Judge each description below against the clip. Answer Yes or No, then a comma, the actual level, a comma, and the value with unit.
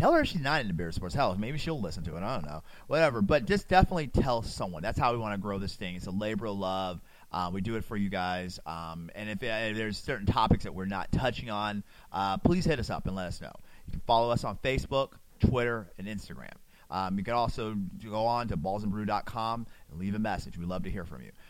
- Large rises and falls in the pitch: No, average, 3.5 semitones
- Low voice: Yes, low, 105 Hz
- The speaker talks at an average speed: No, fast, 255 wpm